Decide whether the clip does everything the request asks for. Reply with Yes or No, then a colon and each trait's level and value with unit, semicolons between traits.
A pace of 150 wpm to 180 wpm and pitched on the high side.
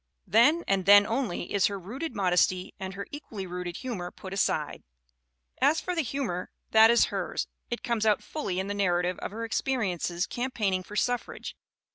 Yes: average, 175 wpm; high, 205 Hz